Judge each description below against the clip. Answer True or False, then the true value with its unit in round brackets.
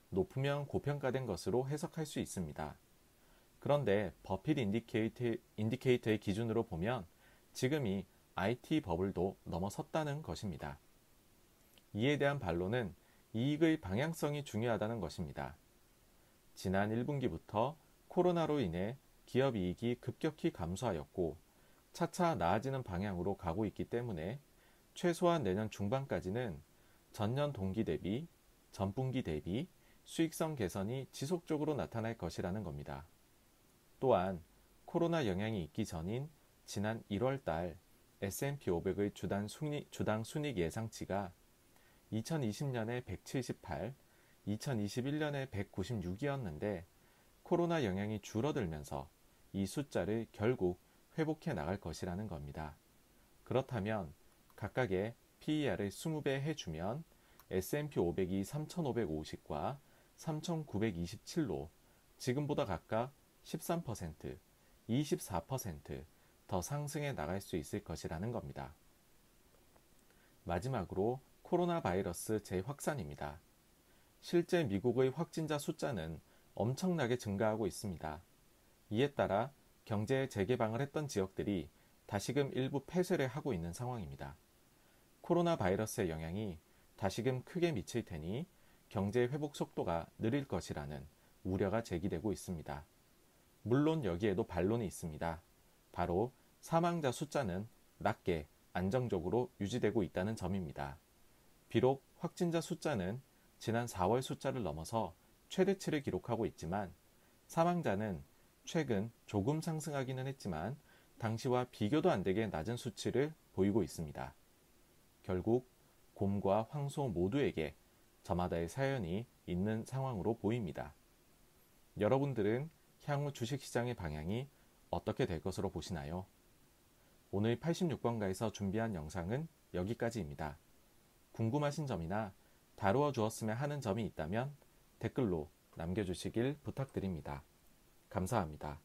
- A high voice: False (115 Hz)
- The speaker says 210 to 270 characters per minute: True (260 characters per minute)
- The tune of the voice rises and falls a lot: True (6.9 semitones)